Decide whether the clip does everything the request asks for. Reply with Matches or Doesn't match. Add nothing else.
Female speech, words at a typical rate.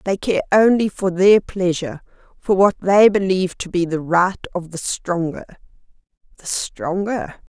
Matches